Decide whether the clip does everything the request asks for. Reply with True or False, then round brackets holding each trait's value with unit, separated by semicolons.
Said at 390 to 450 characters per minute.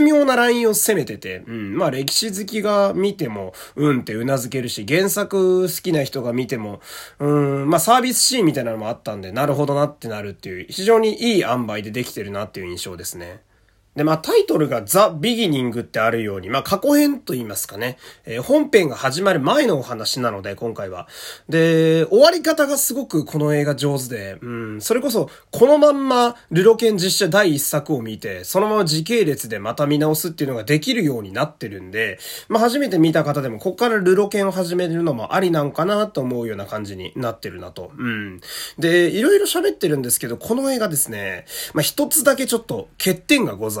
True (420 characters per minute)